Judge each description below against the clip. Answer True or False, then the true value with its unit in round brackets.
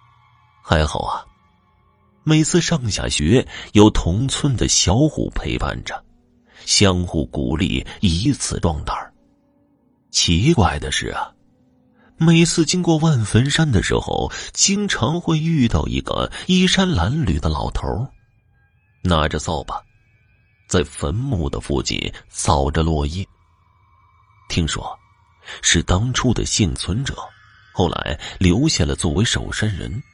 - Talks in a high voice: False (105 Hz)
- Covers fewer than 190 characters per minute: True (175 characters per minute)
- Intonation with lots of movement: True (6.0 semitones)